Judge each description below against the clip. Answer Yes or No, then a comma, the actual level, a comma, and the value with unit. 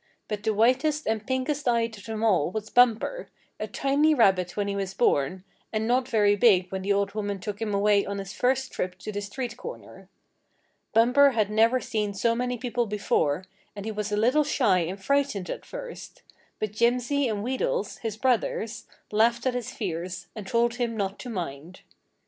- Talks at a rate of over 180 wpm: Yes, average, 190 wpm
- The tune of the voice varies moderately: Yes, average, 3.7 semitones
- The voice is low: No, high, 220 Hz